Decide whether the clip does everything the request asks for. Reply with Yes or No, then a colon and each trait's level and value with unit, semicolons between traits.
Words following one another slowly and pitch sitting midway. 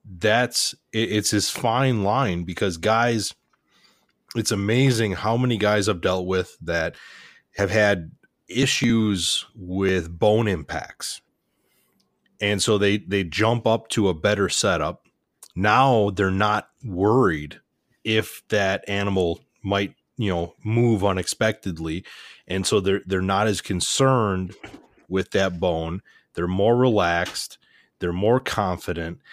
No: slow, 125 wpm; low, 100 Hz